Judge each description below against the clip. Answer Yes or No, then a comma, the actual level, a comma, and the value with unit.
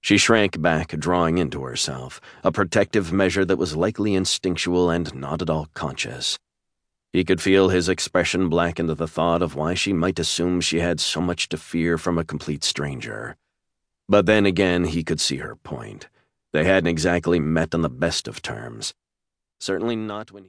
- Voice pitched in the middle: No, very low, 85 Hz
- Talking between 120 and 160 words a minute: No, average, 185 wpm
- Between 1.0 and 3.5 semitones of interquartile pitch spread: Yes, narrow, 2.5 semitones